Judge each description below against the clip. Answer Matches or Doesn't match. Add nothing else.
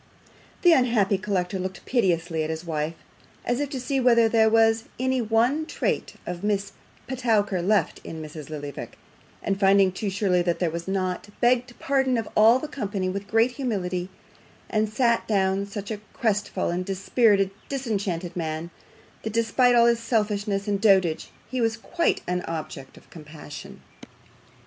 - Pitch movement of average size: Matches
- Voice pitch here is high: Matches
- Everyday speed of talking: Matches